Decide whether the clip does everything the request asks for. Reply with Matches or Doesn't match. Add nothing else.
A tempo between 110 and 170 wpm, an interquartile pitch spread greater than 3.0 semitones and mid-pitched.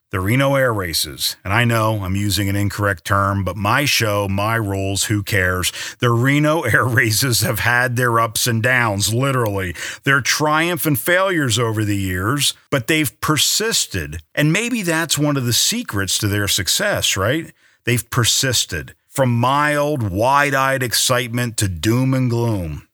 Doesn't match